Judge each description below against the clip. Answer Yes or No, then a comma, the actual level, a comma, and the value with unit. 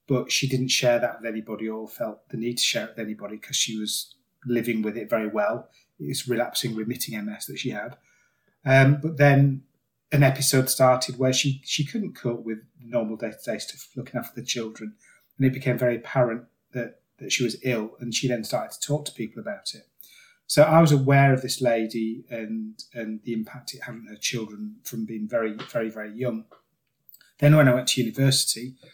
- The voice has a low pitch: Yes, low, 120 Hz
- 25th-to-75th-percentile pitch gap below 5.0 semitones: Yes, average, 3.2 semitones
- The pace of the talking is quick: Yes, fast, 210 wpm